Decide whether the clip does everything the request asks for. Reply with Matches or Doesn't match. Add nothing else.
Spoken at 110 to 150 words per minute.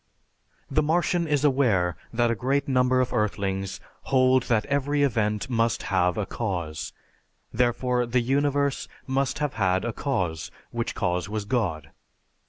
Matches